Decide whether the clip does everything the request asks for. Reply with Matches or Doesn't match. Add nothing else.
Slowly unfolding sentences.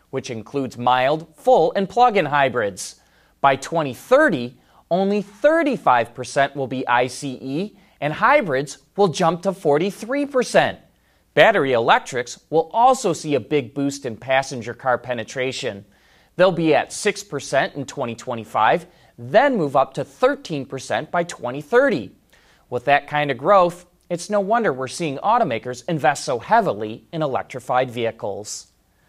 Matches